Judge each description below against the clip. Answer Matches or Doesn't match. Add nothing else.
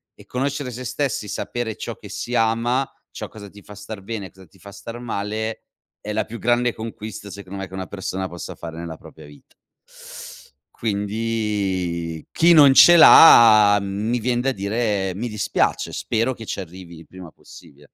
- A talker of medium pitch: Doesn't match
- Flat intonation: Doesn't match